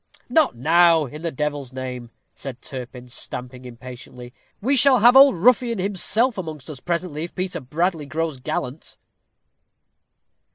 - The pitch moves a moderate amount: No, wide, 6.4 semitones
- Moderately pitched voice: Yes, medium, 155 Hz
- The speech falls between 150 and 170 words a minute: No, slow, 135 wpm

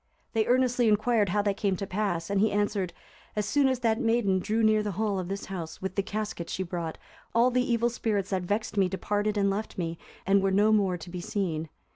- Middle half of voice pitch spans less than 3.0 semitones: Yes, narrow, 2.6 semitones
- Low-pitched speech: No, high, 205 Hz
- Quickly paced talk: Yes, fast, 230 wpm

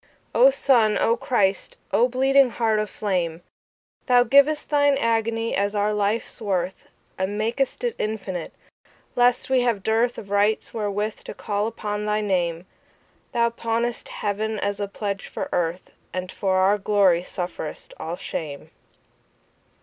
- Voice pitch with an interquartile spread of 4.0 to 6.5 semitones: No, average, 3.2 semitones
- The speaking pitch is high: Yes, high, 210 Hz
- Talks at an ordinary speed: No, slow, 130 wpm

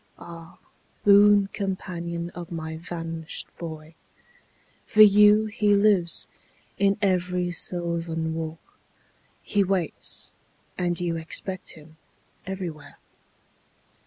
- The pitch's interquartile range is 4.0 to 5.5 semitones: No, average, 3.1 semitones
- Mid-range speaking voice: Yes, medium, 175 Hz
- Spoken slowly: Yes, slow, 95 wpm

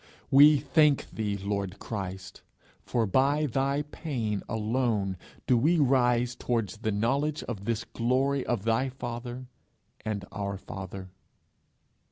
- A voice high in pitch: No, low, 120 Hz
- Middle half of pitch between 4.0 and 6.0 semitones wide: Yes, average, 4.8 semitones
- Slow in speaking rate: Yes, slow, 125 wpm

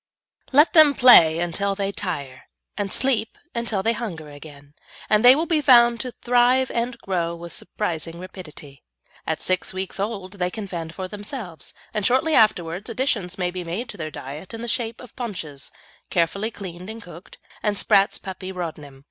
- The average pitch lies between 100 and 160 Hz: No, high, 195 Hz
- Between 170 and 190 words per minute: Yes, average, 175 wpm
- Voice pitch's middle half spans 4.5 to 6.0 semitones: Yes, wide, 5.4 semitones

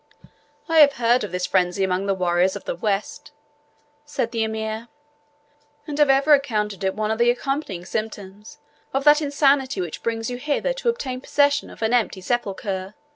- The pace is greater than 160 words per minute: Yes, average, 180 wpm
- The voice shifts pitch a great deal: Yes, wide, 6.1 semitones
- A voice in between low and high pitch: No, high, 225 Hz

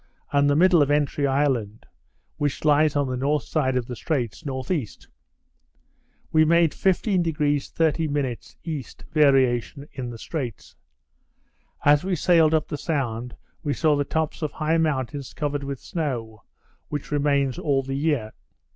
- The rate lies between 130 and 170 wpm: Yes, average, 145 wpm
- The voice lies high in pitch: No, medium, 145 Hz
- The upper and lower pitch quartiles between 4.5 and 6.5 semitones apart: No, average, 2.9 semitones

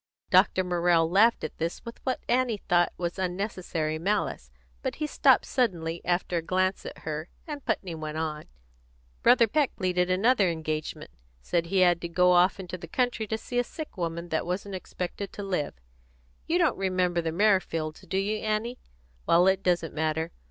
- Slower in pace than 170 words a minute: No, average, 180 wpm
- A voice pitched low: No, medium, 180 Hz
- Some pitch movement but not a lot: Yes, average, 3.8 semitones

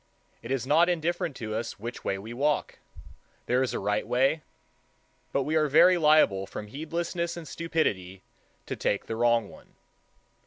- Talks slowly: No, average, 165 wpm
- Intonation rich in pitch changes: Yes, wide, 6.3 semitones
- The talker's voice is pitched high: No, low, 135 Hz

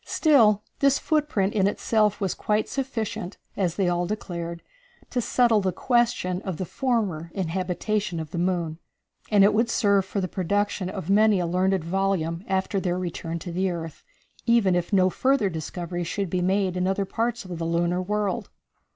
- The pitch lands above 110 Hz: Yes, high, 190 Hz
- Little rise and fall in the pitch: No, average, 3.2 semitones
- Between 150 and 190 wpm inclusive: Yes, average, 175 wpm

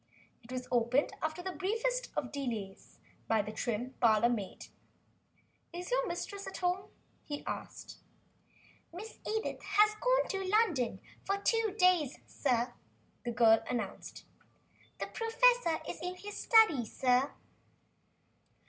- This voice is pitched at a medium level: No, very high, 335 Hz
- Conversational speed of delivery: No, slow, 130 wpm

